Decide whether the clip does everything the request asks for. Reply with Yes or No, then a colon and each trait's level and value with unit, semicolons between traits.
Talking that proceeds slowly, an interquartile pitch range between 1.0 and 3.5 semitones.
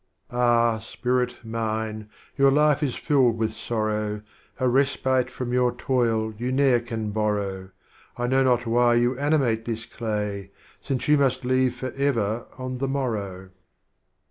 No: average, 145 wpm; average, 2.8 semitones